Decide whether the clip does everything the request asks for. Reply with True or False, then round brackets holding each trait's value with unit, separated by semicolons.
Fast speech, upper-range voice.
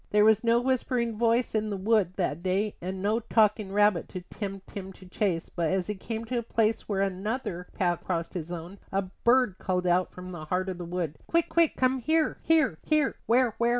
True (225 wpm; 200 Hz)